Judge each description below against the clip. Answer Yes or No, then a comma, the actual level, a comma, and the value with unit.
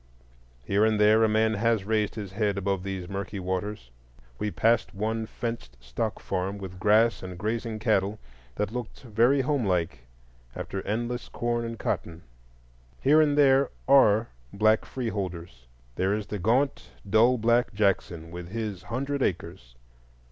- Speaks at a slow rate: No, average, 155 wpm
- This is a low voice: Yes, low, 105 Hz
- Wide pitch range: No, average, 3.3 semitones